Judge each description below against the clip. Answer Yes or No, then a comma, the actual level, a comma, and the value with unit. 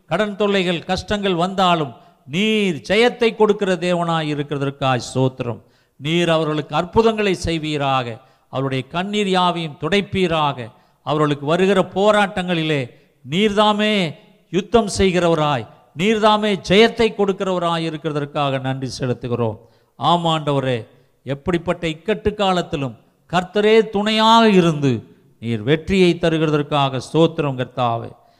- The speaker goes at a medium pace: Yes, average, 90 wpm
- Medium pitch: Yes, medium, 165 Hz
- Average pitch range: No, wide, 6.0 semitones